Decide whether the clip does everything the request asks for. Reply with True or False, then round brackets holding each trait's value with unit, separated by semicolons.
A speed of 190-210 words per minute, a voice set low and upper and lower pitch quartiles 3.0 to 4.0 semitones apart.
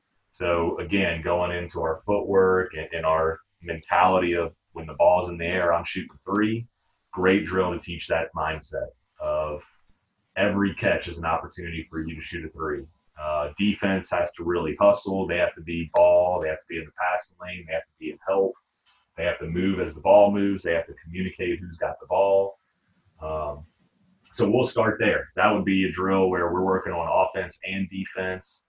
False (205 wpm; 90 Hz; 2.4 semitones)